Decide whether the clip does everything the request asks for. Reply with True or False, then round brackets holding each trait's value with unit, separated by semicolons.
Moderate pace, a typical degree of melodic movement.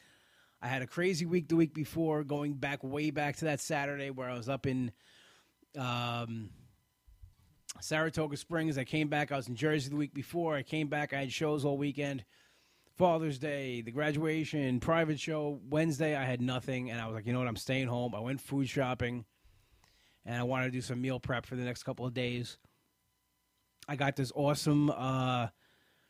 True (195 wpm; 3.3 semitones)